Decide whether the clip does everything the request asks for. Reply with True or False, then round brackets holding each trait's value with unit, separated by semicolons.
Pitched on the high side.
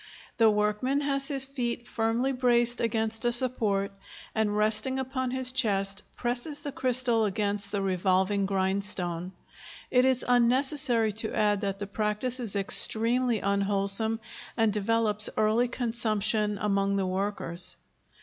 True (220 Hz)